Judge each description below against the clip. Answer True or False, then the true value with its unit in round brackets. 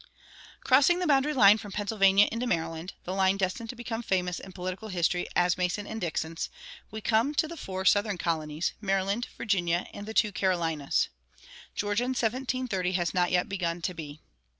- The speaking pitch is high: True (195 Hz)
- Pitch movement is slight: False (3.9 semitones)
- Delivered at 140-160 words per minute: False (175 wpm)